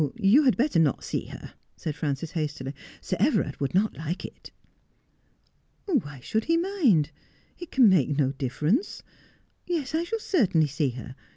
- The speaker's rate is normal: Yes, average, 175 wpm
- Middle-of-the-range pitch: Yes, medium, 180 Hz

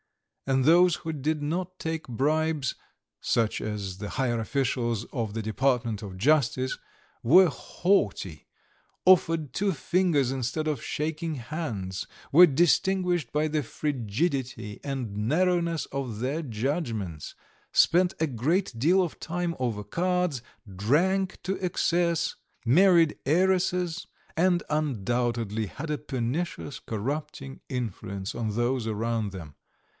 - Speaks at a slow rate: Yes, slow, 120 wpm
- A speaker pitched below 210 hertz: Yes, medium, 140 Hz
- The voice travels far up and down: Yes, wide, 6.5 semitones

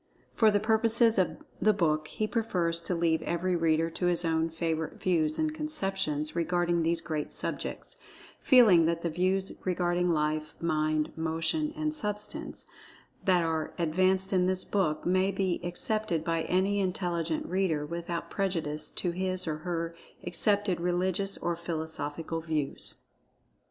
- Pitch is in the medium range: Yes, medium, 175 Hz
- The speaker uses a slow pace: No, average, 145 wpm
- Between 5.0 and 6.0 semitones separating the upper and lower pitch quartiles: No, average, 2.9 semitones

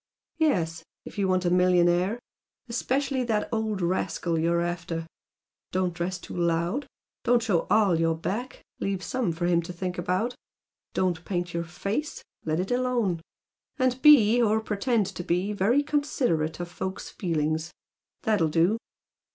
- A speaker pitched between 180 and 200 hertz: Yes, medium, 185 Hz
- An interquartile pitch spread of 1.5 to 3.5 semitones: No, average, 4.7 semitones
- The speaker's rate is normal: Yes, average, 150 wpm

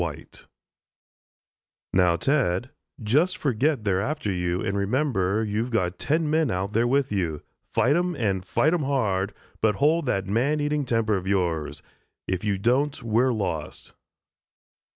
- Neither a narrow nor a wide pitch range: No, wide, 6.9 semitones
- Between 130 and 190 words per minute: Yes, average, 150 wpm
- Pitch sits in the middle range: No, low, 110 Hz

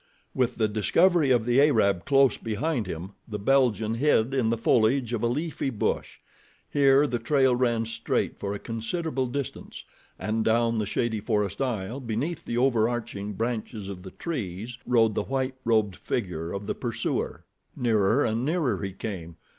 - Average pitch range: Yes, average, 3.8 semitones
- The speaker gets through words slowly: No, average, 165 wpm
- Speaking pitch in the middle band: No, low, 115 Hz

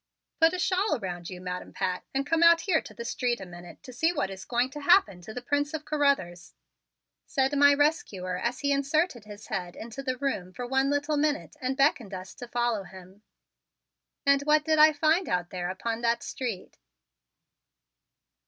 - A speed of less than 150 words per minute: No, average, 190 wpm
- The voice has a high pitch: Yes, very high, 255 Hz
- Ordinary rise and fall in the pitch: No, wide, 7.3 semitones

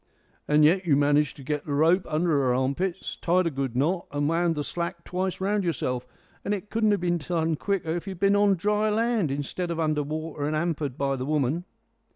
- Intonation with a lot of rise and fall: No, average, 4.1 semitones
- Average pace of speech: No, fast, 220 wpm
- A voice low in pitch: No, medium, 165 Hz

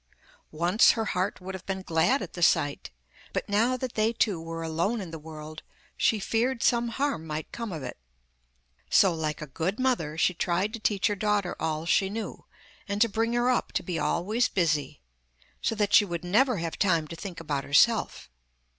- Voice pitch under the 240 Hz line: Yes, high, 190 Hz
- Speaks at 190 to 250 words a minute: Yes, average, 200 wpm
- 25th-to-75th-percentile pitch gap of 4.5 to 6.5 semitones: Yes, wide, 5.6 semitones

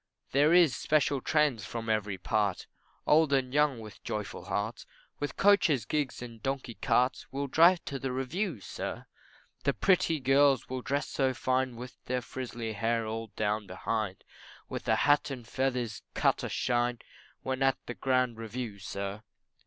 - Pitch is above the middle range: No, low, 125 Hz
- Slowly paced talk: No, average, 160 wpm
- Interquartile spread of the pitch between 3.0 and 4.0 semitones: Yes, average, 3.7 semitones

